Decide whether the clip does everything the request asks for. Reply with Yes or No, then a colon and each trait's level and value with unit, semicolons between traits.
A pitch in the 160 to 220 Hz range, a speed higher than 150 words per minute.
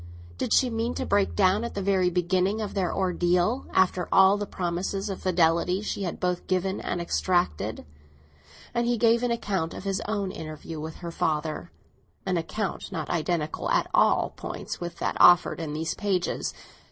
Yes: medium, 185 Hz; average, 175 wpm